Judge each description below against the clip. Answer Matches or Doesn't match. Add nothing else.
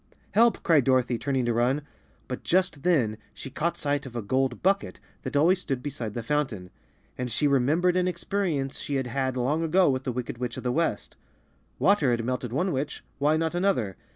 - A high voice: Doesn't match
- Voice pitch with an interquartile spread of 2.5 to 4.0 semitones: Doesn't match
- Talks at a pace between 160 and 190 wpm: Doesn't match